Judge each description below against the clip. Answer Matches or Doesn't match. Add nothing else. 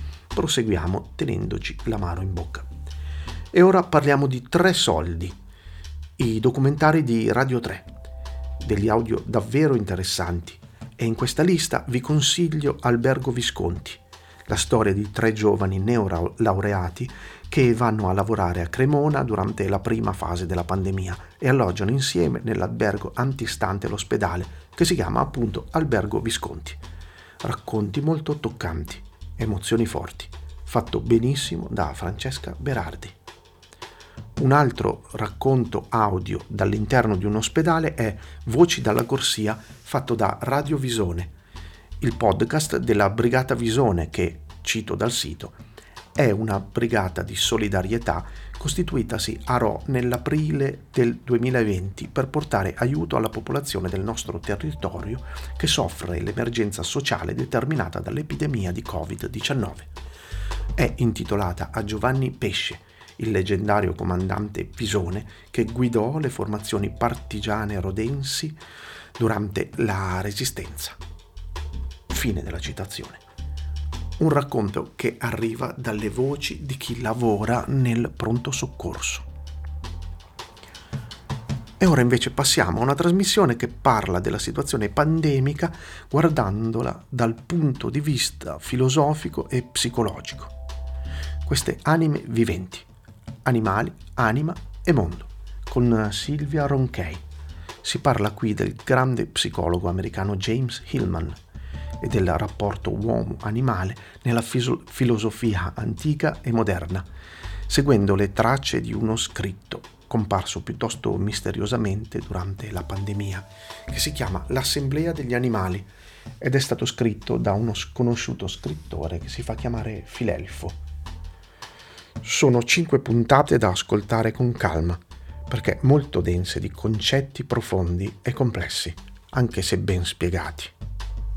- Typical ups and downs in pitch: Doesn't match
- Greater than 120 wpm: Doesn't match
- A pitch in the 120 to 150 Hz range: Doesn't match